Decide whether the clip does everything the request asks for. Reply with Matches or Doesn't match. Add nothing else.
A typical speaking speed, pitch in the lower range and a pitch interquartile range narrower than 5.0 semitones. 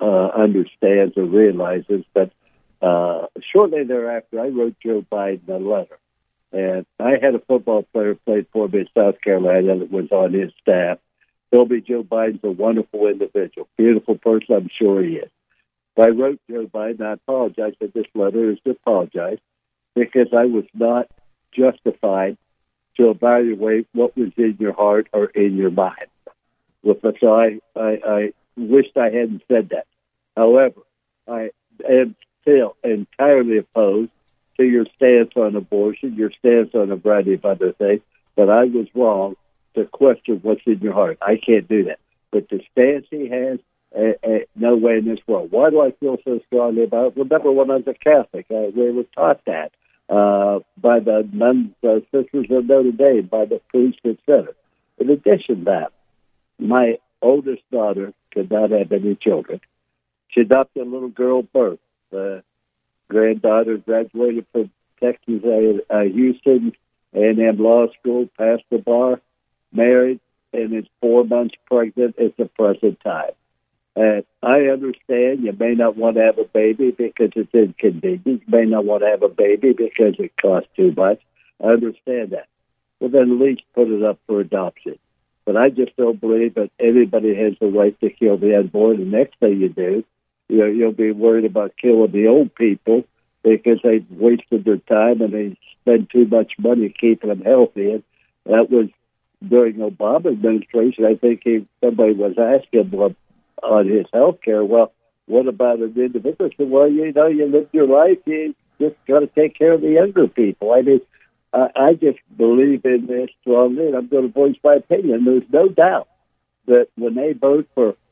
Matches